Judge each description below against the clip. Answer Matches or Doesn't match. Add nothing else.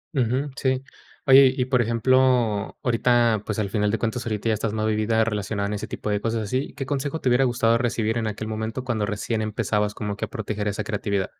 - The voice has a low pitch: Matches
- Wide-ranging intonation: Doesn't match